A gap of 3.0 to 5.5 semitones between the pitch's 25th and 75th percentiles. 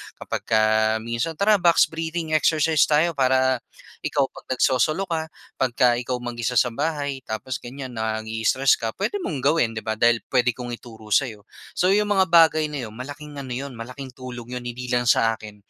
Yes: average, 4.5 semitones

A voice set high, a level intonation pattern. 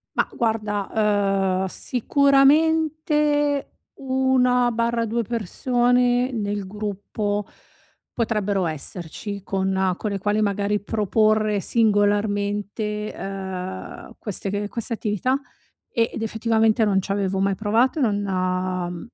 No: high, 210 Hz; average, 3.2 semitones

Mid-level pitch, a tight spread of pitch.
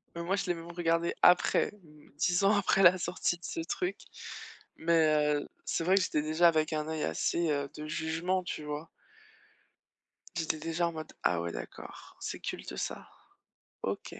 Yes: medium, 170 Hz; narrow, 2.3 semitones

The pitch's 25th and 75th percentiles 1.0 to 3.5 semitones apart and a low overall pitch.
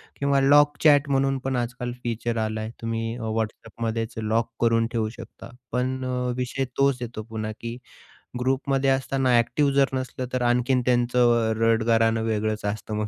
Yes: average, 2.8 semitones; low, 120 Hz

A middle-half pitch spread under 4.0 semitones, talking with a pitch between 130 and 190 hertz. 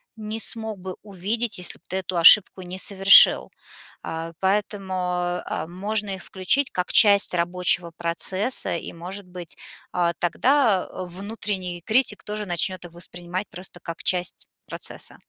Yes: average, 2.8 semitones; medium, 185 Hz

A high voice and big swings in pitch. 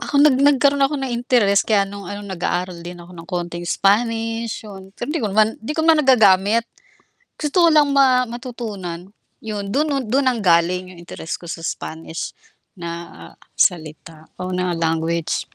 Yes: high, 200 Hz; wide, 6.4 semitones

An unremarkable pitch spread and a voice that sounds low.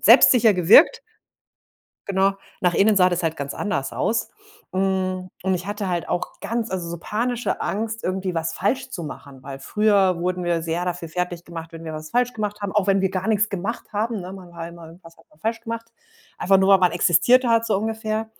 No: average, 4.0 semitones; high, 190 Hz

